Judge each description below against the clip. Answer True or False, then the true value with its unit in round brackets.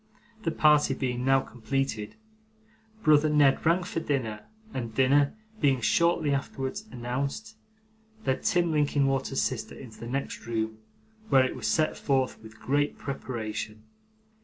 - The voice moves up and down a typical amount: True (3.7 semitones)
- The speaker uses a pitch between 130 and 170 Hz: True (135 Hz)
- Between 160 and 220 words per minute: False (135 wpm)